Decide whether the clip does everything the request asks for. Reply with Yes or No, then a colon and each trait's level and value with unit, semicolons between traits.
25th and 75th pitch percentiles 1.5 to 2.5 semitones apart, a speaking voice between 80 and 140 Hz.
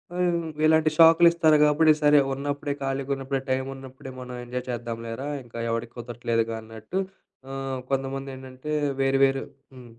No: average, 2.9 semitones; low, 135 Hz